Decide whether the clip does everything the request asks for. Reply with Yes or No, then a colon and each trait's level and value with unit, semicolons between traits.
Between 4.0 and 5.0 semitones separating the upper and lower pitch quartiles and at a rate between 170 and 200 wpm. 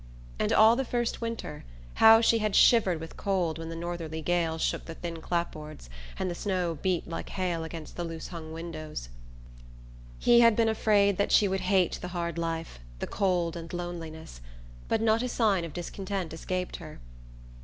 No: average, 3.5 semitones; average, 180 wpm